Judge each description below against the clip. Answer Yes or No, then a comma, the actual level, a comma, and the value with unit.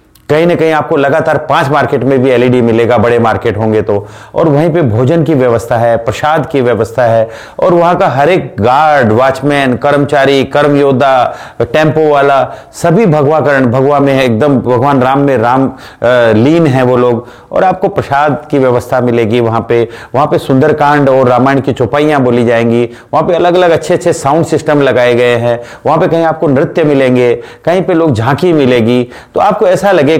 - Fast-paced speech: Yes, fast, 190 wpm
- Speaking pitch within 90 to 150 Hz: Yes, low, 135 Hz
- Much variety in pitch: No, average, 4.0 semitones